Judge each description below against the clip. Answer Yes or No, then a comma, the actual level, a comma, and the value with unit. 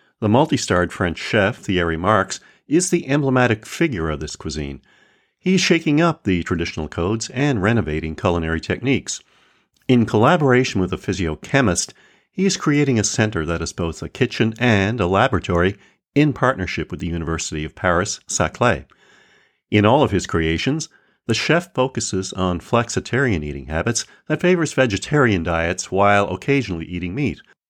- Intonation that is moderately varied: No, wide, 7.2 semitones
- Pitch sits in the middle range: No, low, 105 Hz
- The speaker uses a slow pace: No, average, 150 wpm